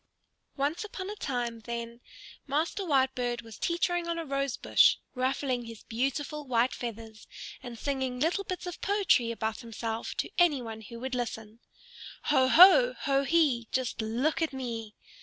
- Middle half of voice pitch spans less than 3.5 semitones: No, average, 4.9 semitones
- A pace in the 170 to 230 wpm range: No, average, 160 wpm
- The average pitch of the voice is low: No, very high, 260 Hz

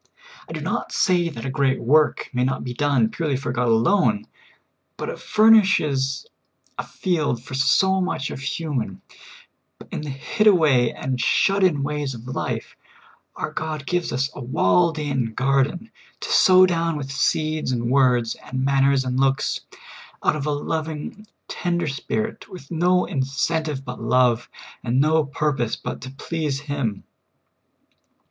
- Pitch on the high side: No, medium, 140 Hz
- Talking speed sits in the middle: Yes, average, 155 wpm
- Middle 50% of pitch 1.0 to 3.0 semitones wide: No, average, 4.0 semitones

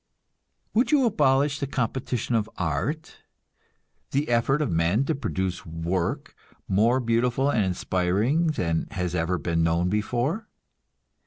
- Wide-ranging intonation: Yes, wide, 7.5 semitones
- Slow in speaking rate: Yes, slow, 130 wpm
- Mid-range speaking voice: No, low, 115 Hz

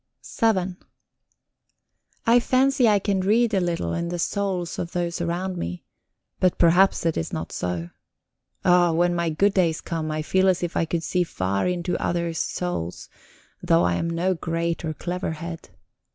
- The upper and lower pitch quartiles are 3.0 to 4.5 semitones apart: No, narrow, 2.4 semitones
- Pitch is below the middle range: No, medium, 175 Hz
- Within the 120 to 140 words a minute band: No, average, 170 wpm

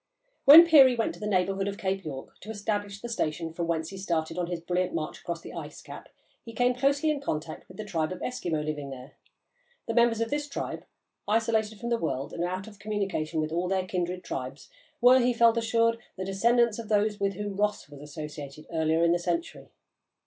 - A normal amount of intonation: No, wide, 5.7 semitones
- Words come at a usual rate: No, fast, 215 wpm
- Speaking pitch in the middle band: No, high, 195 Hz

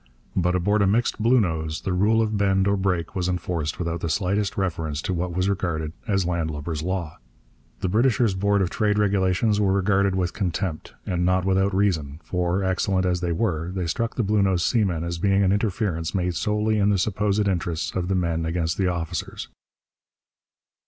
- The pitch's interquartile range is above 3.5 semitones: No, average, 2.8 semitones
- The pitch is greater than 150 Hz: No, very low, 95 Hz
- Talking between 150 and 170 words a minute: No, average, 185 wpm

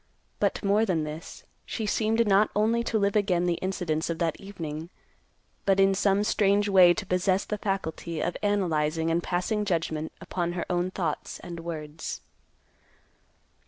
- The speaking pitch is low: No, medium, 185 Hz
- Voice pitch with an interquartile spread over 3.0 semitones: Yes, average, 3.5 semitones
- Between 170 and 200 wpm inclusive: No, average, 160 wpm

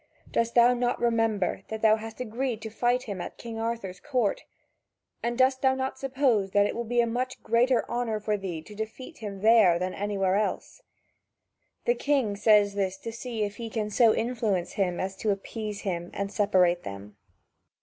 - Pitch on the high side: Yes, high, 220 Hz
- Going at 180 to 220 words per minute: Yes, average, 190 wpm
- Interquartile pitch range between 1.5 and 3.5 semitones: Yes, average, 3.2 semitones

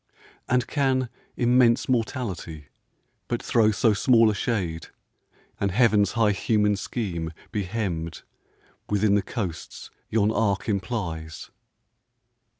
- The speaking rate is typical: No, slow, 110 wpm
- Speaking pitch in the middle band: No, low, 105 Hz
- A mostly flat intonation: No, average, 3.7 semitones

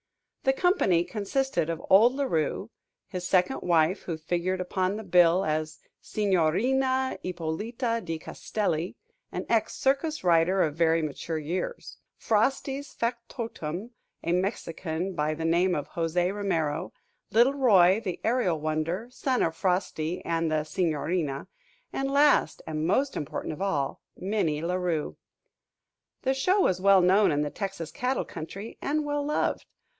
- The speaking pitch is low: No, medium, 185 Hz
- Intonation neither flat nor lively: No, wide, 6.1 semitones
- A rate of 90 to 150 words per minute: Yes, average, 145 wpm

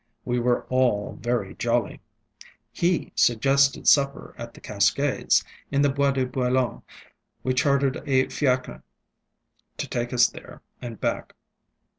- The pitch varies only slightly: Yes, narrow, 2.3 semitones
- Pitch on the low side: Yes, low, 130 Hz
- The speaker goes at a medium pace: No, slow, 130 wpm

